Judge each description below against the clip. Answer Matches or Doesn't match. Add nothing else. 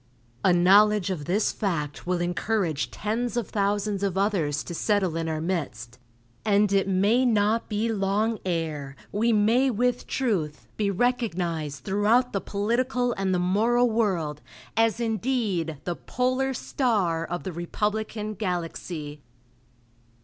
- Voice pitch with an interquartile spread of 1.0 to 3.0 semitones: Doesn't match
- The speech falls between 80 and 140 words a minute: Matches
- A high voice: Matches